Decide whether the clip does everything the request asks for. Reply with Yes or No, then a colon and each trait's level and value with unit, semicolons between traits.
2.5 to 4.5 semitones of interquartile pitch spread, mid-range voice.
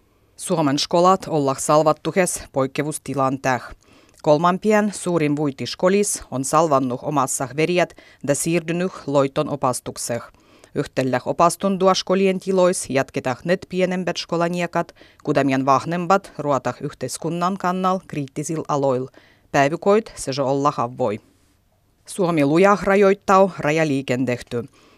No: average, 5.0 semitones; medium, 150 Hz